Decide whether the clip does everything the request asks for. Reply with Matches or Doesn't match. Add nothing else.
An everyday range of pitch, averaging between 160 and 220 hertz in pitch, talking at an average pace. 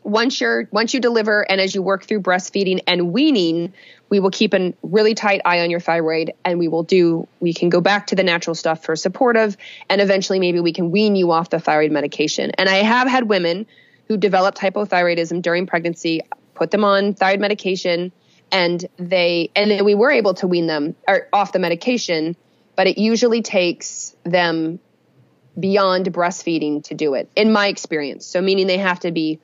Matches